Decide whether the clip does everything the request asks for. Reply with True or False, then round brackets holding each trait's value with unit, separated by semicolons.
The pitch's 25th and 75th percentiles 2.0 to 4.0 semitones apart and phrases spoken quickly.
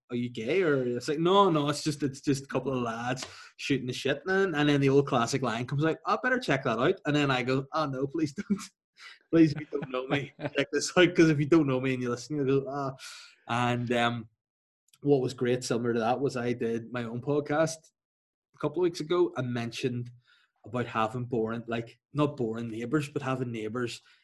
True (3.6 semitones; 230 wpm)